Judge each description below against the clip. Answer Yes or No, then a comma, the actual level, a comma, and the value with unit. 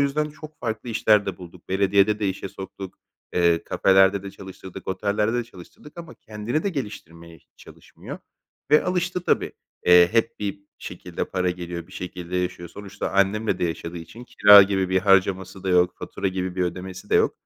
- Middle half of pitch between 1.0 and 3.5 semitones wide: Yes, average, 2.9 semitones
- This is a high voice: No, very low, 95 Hz